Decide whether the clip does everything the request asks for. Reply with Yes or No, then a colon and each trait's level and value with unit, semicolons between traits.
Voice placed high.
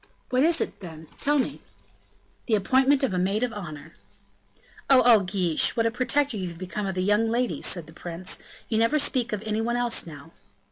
Yes: high, 215 Hz